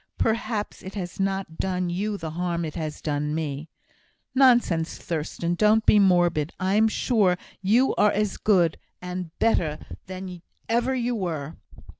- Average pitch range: Yes, average, 4.3 semitones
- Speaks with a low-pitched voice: No, medium, 185 Hz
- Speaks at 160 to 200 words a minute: No, average, 145 wpm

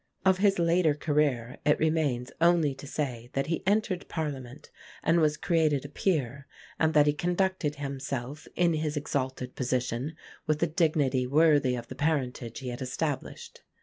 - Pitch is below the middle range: No, medium, 150 Hz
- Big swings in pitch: No, average, 3.7 semitones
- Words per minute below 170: Yes, average, 160 wpm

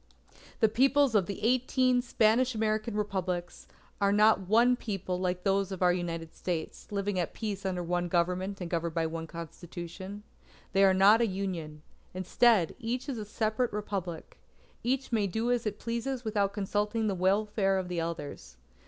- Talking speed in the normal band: Yes, average, 170 wpm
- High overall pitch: Yes, high, 200 Hz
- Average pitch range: Yes, average, 3.7 semitones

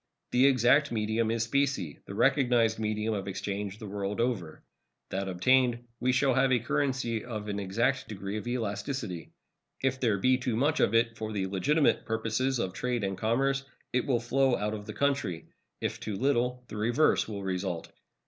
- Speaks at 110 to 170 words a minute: No, average, 180 wpm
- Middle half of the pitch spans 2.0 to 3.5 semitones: No, average, 3.9 semitones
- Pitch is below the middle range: Yes, low, 115 Hz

